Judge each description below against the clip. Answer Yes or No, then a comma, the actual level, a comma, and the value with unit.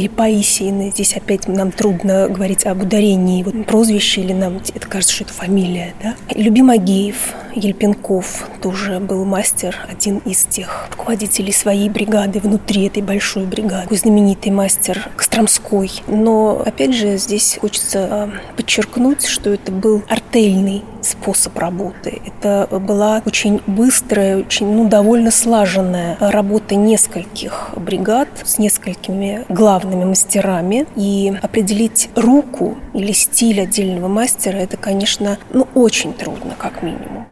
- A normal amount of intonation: No, narrow, 2.1 semitones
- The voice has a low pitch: No, high, 205 Hz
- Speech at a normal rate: Yes, average, 125 wpm